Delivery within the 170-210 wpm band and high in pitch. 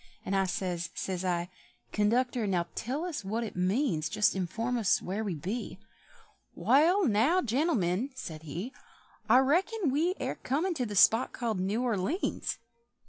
No: average, 160 wpm; high, 225 Hz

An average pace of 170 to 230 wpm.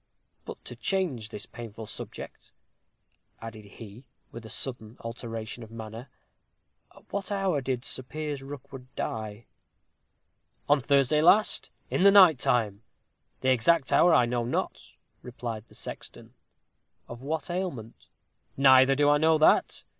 No: average, 140 wpm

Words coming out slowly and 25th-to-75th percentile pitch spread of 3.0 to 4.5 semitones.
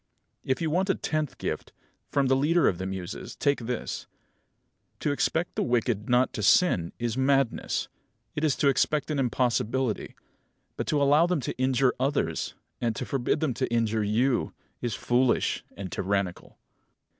No: average, 165 wpm; average, 4.1 semitones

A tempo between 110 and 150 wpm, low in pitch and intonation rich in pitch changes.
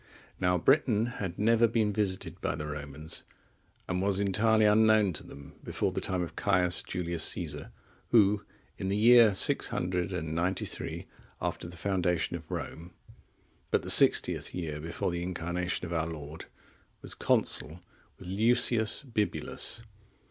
No: average, 140 wpm; very low, 90 Hz; average, 3.8 semitones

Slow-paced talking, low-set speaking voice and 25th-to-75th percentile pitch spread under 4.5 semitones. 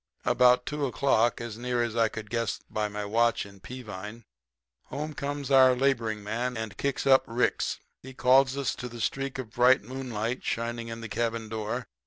No: average, 185 wpm; low, 120 Hz; average, 2.8 semitones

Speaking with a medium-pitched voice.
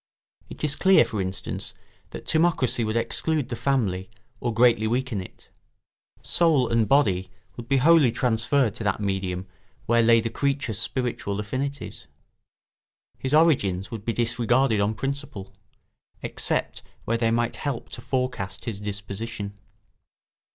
No: low, 115 Hz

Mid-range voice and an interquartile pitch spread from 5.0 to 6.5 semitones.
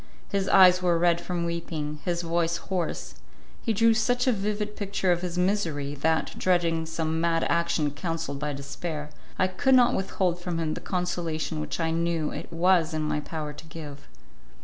No: medium, 170 Hz; narrow, 2.6 semitones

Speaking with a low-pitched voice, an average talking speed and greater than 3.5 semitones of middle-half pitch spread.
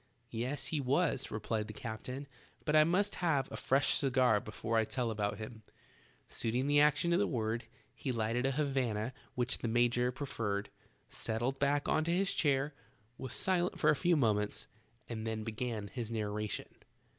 Yes: low, 125 Hz; average, 170 wpm; average, 4.6 semitones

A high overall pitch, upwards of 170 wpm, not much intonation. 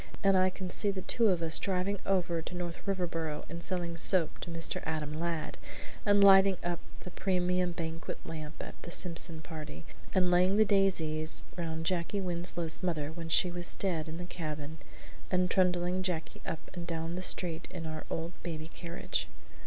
No: medium, 175 Hz; average, 180 wpm; narrow, 2.2 semitones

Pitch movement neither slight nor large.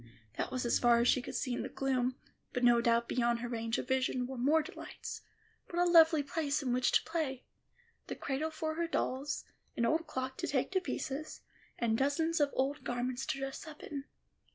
Yes: average, 4.0 semitones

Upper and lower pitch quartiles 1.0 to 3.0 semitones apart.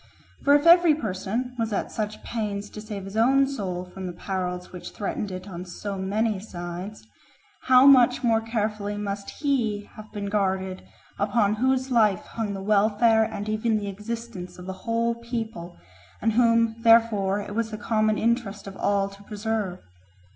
Yes: average, 2.7 semitones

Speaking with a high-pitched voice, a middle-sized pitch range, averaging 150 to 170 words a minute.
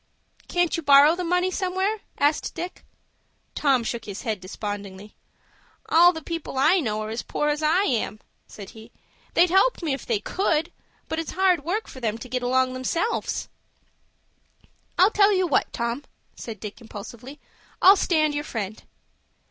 No: very high, 290 Hz; wide, 7.4 semitones; average, 165 wpm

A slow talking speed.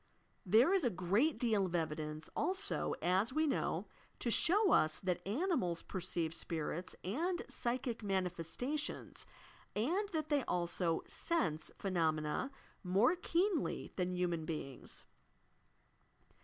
Yes: slow, 115 wpm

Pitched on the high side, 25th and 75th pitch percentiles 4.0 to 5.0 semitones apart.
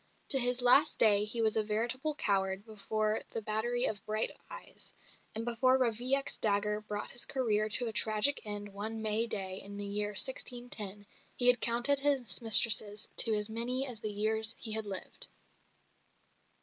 No: high, 220 Hz; average, 2.7 semitones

